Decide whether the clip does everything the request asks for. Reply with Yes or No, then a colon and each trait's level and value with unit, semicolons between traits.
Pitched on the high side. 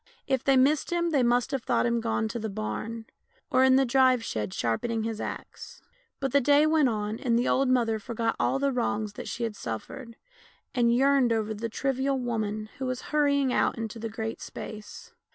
Yes: high, 240 Hz